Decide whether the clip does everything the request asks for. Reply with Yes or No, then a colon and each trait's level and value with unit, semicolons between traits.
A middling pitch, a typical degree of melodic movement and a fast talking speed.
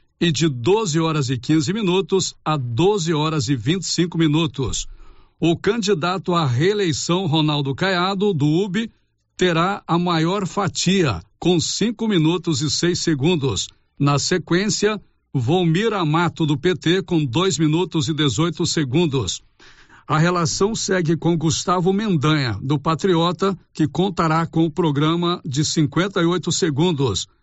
No: medium, 165 Hz; average, 3.0 semitones; average, 140 wpm